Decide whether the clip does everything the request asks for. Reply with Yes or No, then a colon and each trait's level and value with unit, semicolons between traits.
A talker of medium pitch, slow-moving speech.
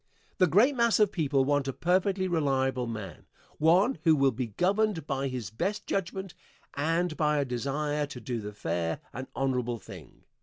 No: medium, 145 Hz; average, 175 wpm